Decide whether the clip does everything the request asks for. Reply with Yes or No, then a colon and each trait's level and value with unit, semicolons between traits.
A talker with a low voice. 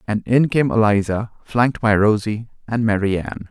Yes: low, 110 Hz